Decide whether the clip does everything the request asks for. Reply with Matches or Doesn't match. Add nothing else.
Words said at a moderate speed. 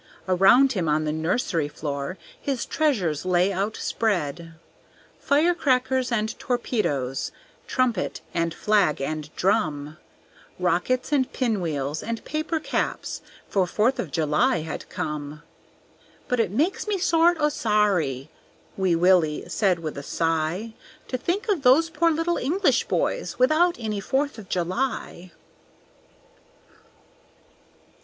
Doesn't match